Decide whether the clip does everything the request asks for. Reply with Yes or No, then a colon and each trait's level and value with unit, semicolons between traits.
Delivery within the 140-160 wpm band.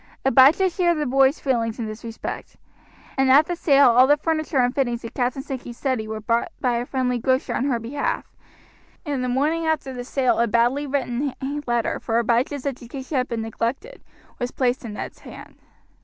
No: average, 190 wpm